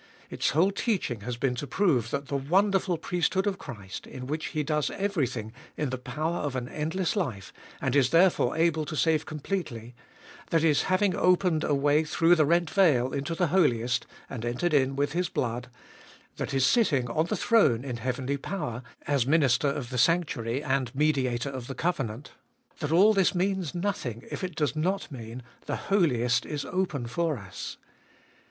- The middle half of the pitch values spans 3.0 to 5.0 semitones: No, wide, 5.5 semitones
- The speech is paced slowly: No, average, 185 wpm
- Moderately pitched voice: Yes, medium, 145 Hz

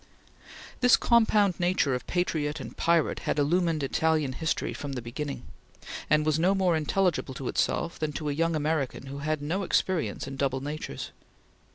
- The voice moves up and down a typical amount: Yes, average, 3.6 semitones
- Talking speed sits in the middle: Yes, average, 170 wpm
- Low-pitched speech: No, medium, 155 Hz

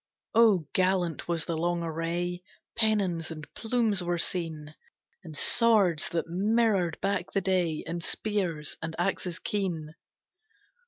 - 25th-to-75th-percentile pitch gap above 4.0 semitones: No, average, 3.3 semitones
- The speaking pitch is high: No, medium, 175 Hz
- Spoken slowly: Yes, slow, 125 wpm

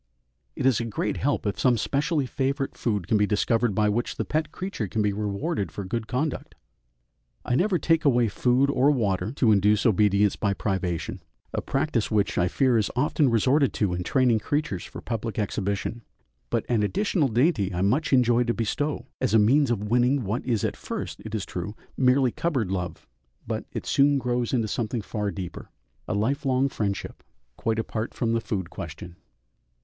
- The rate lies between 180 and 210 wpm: Yes, average, 185 wpm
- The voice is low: Yes, low, 115 Hz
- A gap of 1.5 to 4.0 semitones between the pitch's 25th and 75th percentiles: No, average, 4.4 semitones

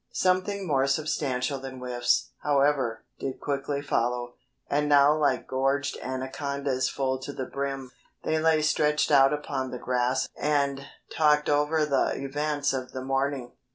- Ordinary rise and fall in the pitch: No, narrow, 2.1 semitones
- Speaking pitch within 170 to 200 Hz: No, medium, 140 Hz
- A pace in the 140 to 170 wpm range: Yes, average, 145 wpm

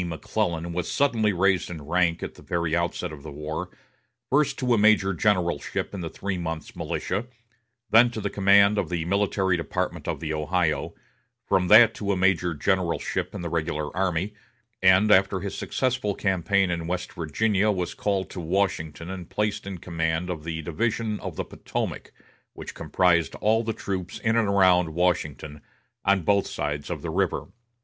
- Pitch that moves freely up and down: No, average, 3.4 semitones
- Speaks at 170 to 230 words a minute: Yes, average, 175 wpm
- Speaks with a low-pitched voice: Yes, very low, 90 Hz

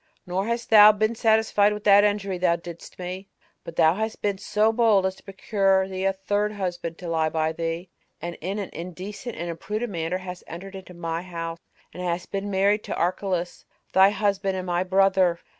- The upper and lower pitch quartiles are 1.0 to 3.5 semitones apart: Yes, average, 2.8 semitones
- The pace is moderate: Yes, average, 195 wpm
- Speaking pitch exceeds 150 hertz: Yes, high, 190 Hz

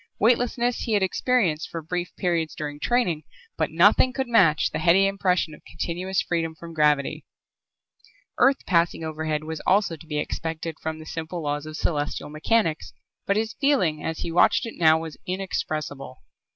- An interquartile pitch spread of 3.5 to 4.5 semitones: Yes, average, 3.9 semitones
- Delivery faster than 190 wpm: No, average, 165 wpm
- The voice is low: No, medium, 165 Hz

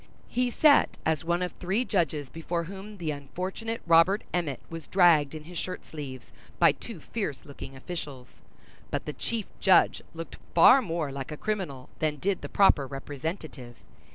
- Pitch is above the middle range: No, medium, 165 Hz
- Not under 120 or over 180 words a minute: Yes, average, 165 wpm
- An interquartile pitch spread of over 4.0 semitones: Yes, average, 4.7 semitones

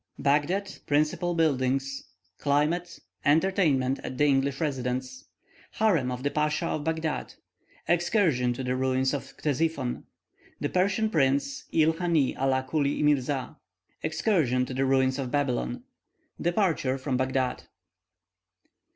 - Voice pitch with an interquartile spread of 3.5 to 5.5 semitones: Yes, average, 3.8 semitones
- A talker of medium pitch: Yes, medium, 145 Hz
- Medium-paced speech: No, slow, 120 wpm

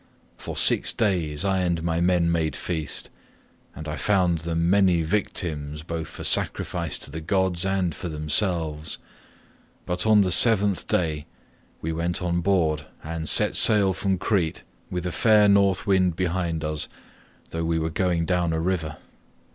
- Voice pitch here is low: Yes, very low, 85 Hz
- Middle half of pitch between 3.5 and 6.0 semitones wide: No, average, 2.8 semitones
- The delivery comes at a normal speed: Yes, average, 160 wpm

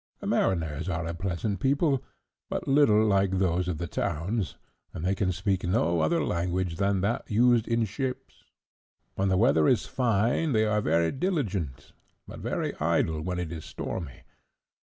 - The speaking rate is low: No, average, 165 wpm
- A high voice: No, very low, 95 Hz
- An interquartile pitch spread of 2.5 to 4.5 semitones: No, average, 5.1 semitones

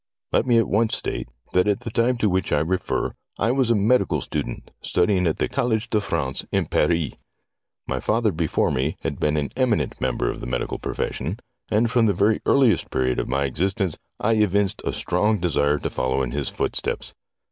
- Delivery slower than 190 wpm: No, average, 200 wpm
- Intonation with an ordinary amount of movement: No, wide, 7.0 semitones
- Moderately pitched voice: No, very low, 95 Hz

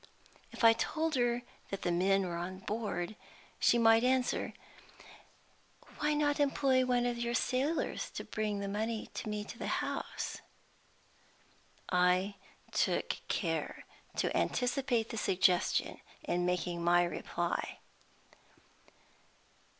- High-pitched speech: Yes, high, 225 Hz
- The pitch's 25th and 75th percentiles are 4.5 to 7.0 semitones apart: Yes, average, 5.1 semitones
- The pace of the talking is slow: Yes, slow, 120 wpm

